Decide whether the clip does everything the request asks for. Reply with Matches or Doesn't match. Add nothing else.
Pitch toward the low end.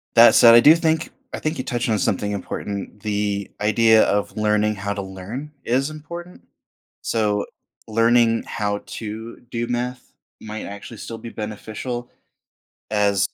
Matches